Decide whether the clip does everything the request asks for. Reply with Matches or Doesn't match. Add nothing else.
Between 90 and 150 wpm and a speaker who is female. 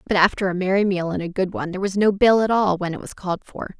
Doesn't match